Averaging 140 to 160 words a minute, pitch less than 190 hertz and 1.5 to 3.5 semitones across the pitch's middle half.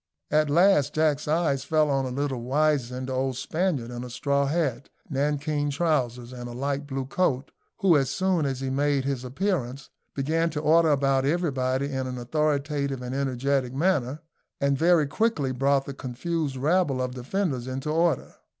No: average, 170 wpm; medium, 140 Hz; average, 2.9 semitones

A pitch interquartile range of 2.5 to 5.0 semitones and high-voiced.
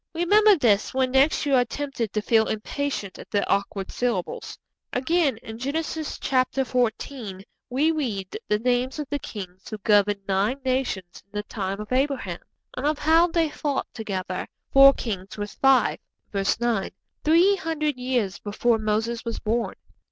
No: wide, 5.4 semitones; high, 245 Hz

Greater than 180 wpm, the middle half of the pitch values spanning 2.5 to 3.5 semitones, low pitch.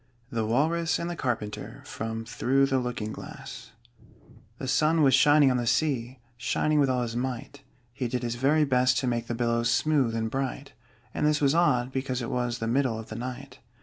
Yes: average, 200 wpm; average, 2.9 semitones; low, 125 Hz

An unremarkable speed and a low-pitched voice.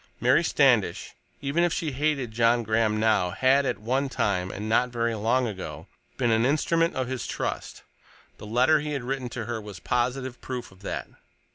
Yes: average, 175 wpm; low, 120 Hz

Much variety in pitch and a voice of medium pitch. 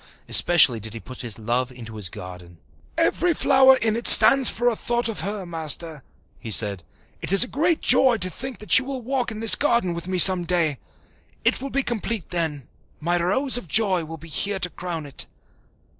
Yes: wide, 8.3 semitones; medium, 180 Hz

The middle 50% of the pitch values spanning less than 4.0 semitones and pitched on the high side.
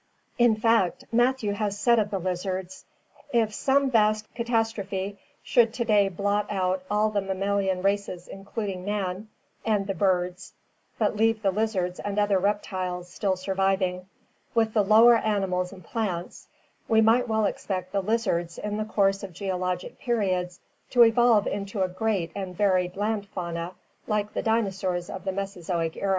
Yes: average, 2.8 semitones; high, 200 Hz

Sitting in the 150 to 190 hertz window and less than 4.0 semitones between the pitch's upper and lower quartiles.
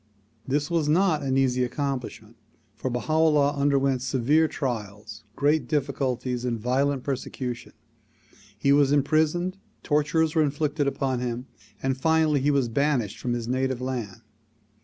No: low, 135 Hz; average, 3.1 semitones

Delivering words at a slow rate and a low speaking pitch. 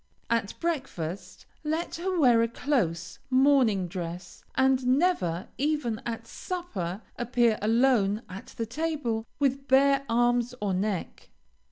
No: slow, 125 wpm; high, 240 Hz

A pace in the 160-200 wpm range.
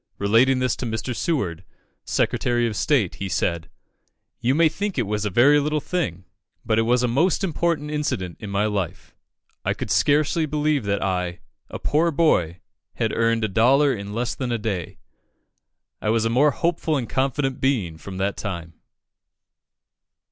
Yes: average, 170 wpm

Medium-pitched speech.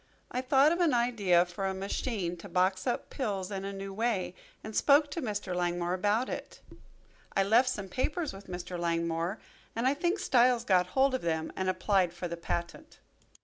No: high, 195 Hz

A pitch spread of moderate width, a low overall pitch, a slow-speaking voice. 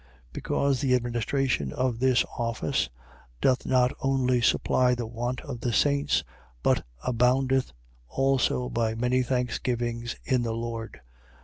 No: narrow, 1.8 semitones; low, 125 Hz; slow, 130 wpm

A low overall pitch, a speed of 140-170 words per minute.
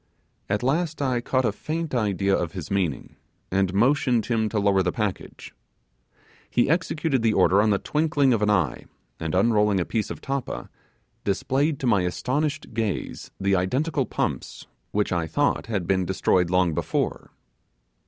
Yes: low, 105 Hz; average, 165 wpm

